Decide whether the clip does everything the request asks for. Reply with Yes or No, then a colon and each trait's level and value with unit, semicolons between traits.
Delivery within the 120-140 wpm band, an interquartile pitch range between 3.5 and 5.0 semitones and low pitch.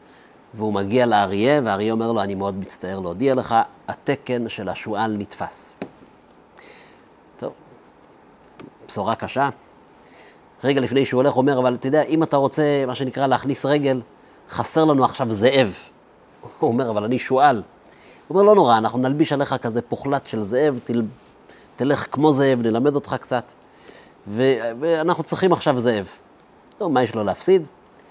No: fast, 150 wpm; average, 4.1 semitones; low, 125 Hz